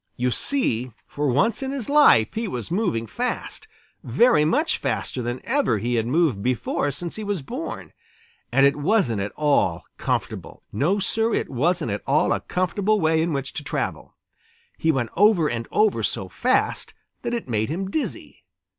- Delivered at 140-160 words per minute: No, average, 175 wpm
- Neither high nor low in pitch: Yes, medium, 155 Hz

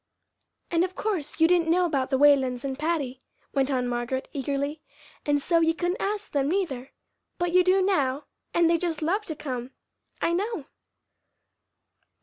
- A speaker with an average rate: Yes, average, 165 wpm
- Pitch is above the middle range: Yes, very high, 310 Hz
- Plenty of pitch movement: No, average, 4.6 semitones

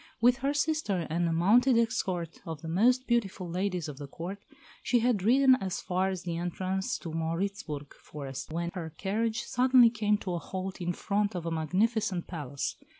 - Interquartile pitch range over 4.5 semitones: Yes, average, 5.2 semitones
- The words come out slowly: No, average, 190 wpm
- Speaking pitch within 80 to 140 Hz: No, high, 190 Hz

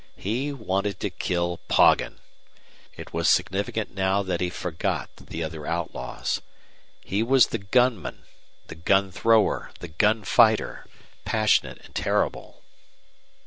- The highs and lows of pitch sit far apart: No, average, 3.9 semitones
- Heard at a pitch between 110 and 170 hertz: No, low, 100 Hz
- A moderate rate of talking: No, slow, 125 wpm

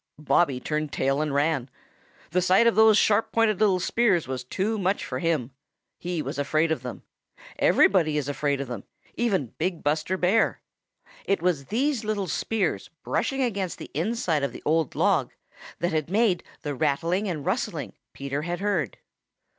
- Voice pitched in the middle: Yes, medium, 170 Hz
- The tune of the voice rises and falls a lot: Yes, wide, 5.8 semitones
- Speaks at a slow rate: No, average, 170 wpm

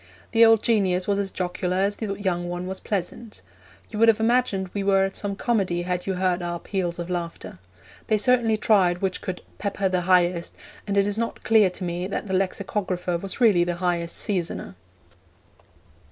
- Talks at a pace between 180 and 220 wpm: Yes, average, 190 wpm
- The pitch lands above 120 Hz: Yes, high, 190 Hz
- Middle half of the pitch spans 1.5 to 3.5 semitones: Yes, narrow, 2.6 semitones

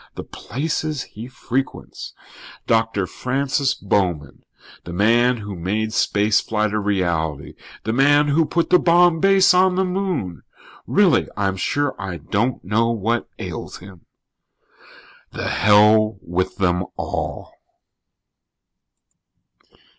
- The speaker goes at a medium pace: No, slow, 115 wpm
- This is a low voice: Yes, low, 110 Hz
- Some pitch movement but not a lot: No, wide, 6.6 semitones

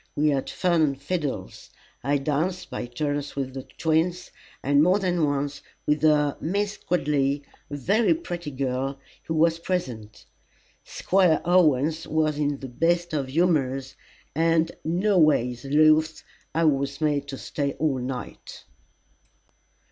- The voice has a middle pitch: Yes, medium, 150 Hz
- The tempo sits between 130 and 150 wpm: Yes, average, 140 wpm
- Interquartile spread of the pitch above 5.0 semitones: No, average, 3.3 semitones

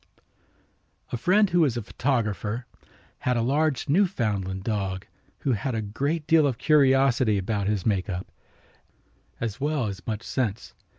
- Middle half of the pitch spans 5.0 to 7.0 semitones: Yes, wide, 5.5 semitones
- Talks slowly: No, average, 150 wpm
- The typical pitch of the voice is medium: No, low, 120 Hz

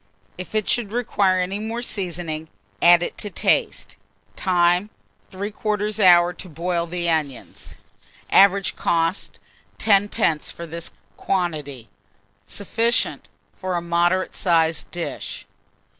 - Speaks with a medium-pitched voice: Yes, medium, 180 Hz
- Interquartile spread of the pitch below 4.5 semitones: Yes, average, 3.0 semitones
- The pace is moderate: No, slow, 115 wpm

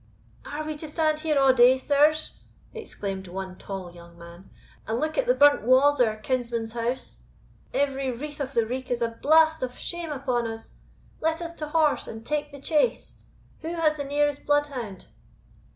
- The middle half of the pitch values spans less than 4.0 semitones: No, average, 4.7 semitones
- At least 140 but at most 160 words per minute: No, average, 185 wpm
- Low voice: No, very high, 275 Hz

